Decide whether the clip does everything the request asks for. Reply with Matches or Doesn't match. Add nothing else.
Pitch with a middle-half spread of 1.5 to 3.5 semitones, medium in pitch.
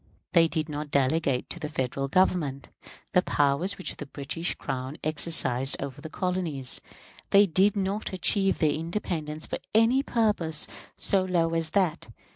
Doesn't match